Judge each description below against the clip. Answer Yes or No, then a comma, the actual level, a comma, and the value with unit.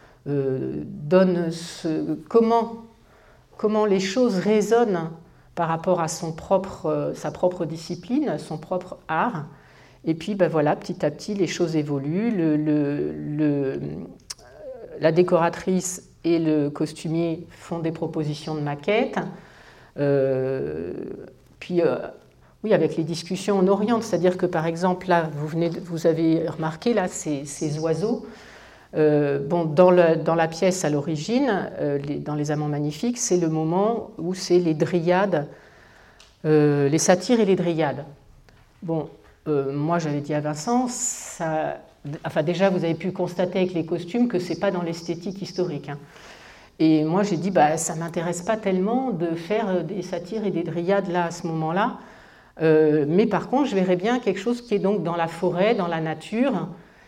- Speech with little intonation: No, average, 3.7 semitones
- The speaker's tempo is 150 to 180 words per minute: Yes, average, 170 wpm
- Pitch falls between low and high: Yes, medium, 170 Hz